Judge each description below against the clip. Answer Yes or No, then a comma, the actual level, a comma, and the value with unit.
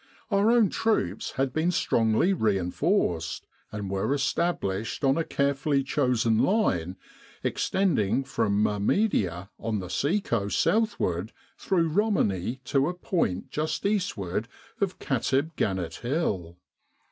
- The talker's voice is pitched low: Yes, low, 130 Hz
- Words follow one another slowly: Yes, slow, 125 wpm